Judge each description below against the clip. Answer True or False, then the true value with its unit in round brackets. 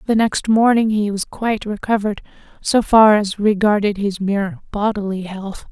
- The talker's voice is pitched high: True (205 Hz)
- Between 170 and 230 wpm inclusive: False (155 wpm)